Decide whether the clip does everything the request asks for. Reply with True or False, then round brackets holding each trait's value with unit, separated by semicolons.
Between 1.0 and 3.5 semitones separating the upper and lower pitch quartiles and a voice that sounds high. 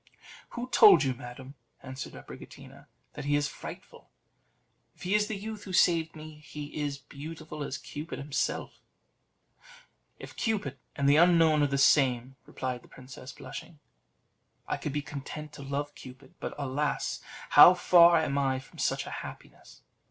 False (3.1 semitones; 145 Hz)